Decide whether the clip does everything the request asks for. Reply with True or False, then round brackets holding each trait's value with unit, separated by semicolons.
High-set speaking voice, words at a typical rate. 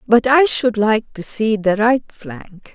True (220 Hz; 195 wpm)